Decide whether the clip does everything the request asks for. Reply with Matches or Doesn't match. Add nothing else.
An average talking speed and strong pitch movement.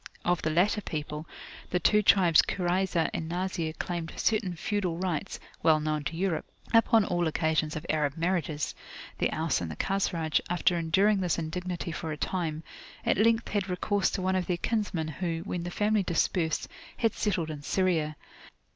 Doesn't match